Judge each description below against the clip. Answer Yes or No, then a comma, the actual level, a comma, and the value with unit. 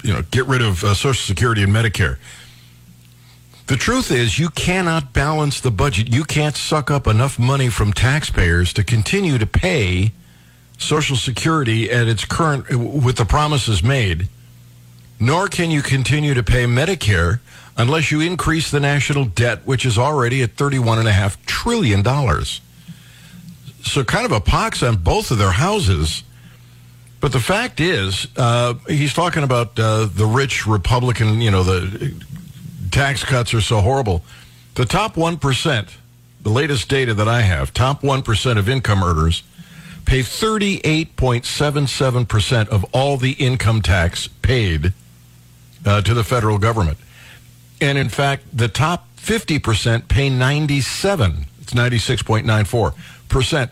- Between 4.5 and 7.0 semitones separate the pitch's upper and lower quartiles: Yes, wide, 5.5 semitones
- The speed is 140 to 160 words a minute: Yes, average, 145 wpm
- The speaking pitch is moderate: No, low, 120 Hz